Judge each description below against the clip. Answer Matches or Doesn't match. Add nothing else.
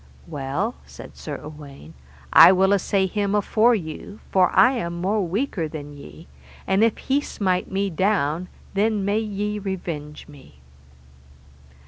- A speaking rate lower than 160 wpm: Matches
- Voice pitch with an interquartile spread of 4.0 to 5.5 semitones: Matches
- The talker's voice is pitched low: Doesn't match